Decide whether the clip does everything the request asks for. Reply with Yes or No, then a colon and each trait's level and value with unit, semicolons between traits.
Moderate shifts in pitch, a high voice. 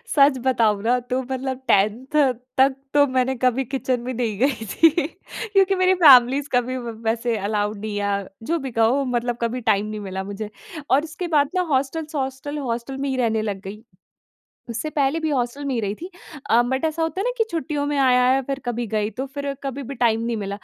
Yes: average, 3.8 semitones; very high, 255 Hz